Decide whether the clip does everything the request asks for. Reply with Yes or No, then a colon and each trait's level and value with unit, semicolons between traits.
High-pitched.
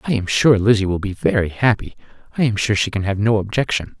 No: low, 110 Hz